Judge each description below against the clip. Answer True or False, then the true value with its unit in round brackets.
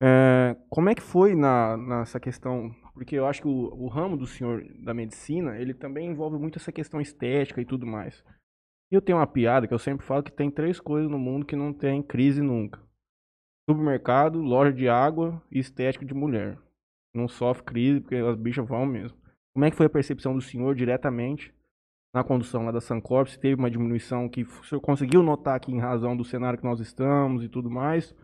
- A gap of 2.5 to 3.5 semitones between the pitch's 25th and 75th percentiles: True (3.0 semitones)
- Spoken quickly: True (210 wpm)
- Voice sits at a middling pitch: False (130 Hz)